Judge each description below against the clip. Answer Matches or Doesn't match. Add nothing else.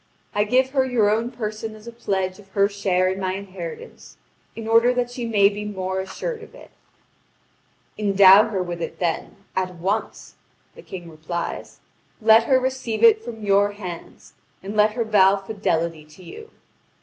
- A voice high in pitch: Matches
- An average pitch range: Matches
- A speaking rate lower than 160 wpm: Doesn't match